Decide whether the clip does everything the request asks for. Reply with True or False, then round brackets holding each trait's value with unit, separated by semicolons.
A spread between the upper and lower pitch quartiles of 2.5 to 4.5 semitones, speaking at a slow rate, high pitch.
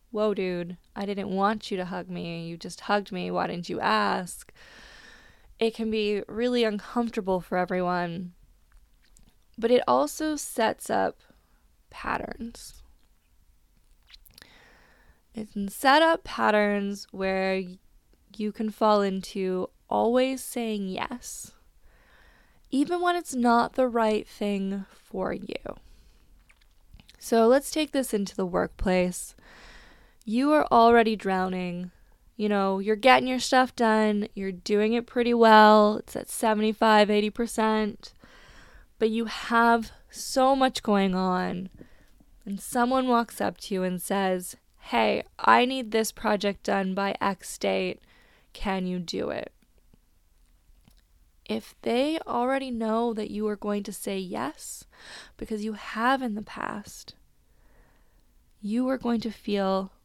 True (4.2 semitones; 130 wpm; 210 Hz)